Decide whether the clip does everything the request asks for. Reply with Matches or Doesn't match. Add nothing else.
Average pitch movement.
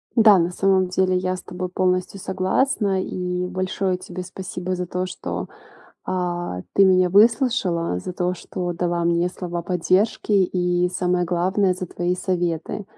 Doesn't match